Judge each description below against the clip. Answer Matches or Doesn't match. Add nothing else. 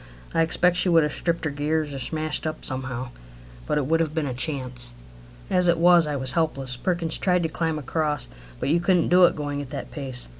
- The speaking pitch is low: Doesn't match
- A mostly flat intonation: Doesn't match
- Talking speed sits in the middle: Doesn't match